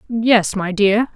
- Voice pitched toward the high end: Yes, high, 215 Hz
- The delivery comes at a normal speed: Yes, average, 155 wpm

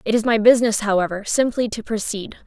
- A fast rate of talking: No, average, 195 wpm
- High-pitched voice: Yes, high, 220 Hz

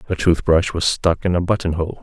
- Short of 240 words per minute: Yes, fast, 205 wpm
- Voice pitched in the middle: No, very low, 85 Hz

